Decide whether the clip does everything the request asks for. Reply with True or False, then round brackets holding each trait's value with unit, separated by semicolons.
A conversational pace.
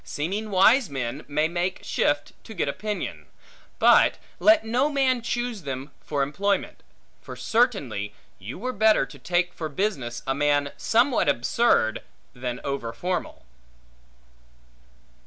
False (125 wpm)